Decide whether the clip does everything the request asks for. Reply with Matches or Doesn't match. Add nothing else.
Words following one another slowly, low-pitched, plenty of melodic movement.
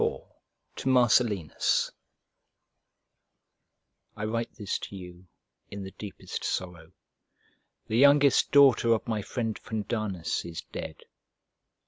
Doesn't match